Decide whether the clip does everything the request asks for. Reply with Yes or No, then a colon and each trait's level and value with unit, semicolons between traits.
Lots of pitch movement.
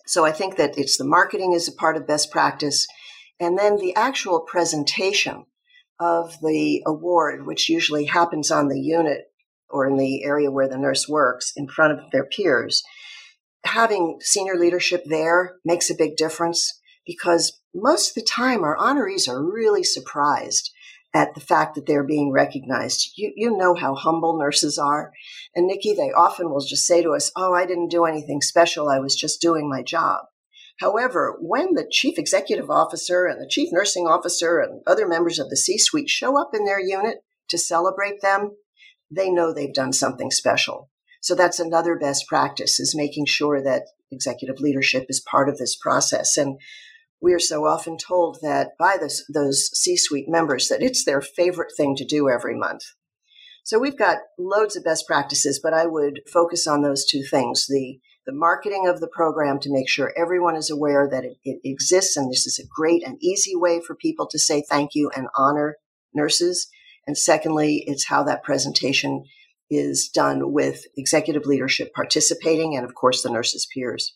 No: average, 4.0 semitones